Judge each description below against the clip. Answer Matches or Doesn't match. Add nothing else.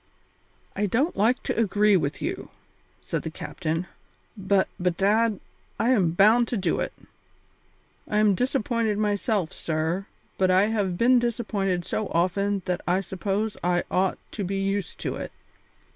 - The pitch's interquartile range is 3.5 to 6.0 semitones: Doesn't match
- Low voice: Doesn't match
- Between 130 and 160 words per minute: Matches